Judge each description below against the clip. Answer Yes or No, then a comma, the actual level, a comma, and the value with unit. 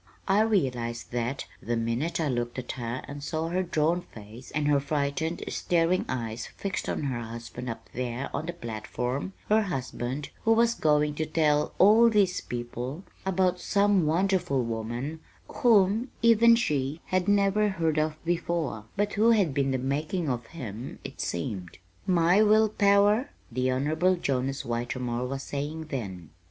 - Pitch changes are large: Yes, wide, 7.0 semitones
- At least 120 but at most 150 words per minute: No, average, 160 wpm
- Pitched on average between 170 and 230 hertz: No, medium, 150 Hz